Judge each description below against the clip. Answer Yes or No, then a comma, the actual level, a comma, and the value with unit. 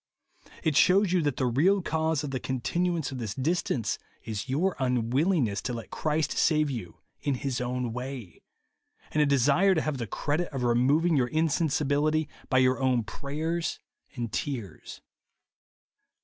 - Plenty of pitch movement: No, average, 4.1 semitones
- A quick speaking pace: No, average, 160 wpm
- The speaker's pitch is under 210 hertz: Yes, medium, 140 Hz